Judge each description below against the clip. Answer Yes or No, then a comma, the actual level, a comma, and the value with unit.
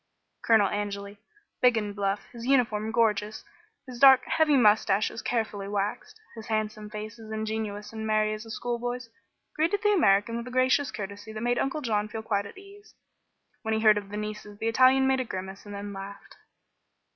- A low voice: No, high, 220 Hz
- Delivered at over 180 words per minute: Yes, average, 190 wpm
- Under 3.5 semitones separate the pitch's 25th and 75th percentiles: Yes, average, 2.9 semitones